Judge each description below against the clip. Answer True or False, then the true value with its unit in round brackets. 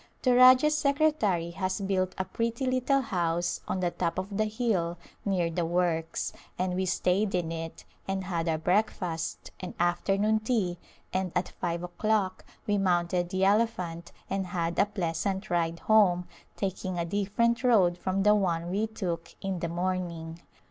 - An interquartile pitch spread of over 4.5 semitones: False (3.3 semitones)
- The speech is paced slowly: False (160 wpm)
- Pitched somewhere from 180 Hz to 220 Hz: True (185 Hz)